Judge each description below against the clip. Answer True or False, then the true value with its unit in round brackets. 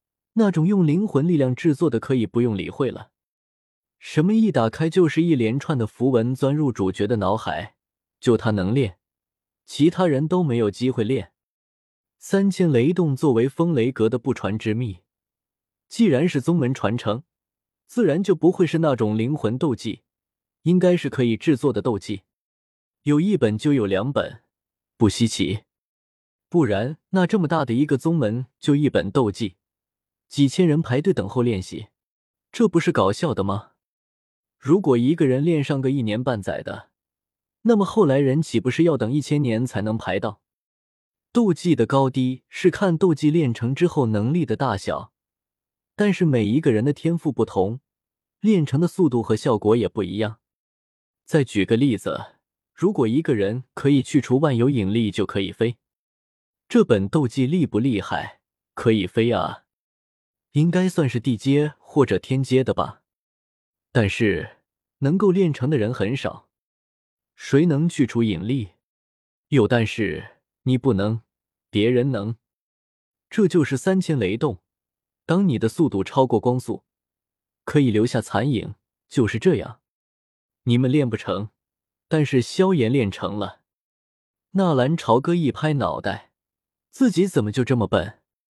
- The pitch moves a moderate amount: False (6.6 semitones)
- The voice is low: True (130 Hz)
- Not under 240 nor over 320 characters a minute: False (225 characters per minute)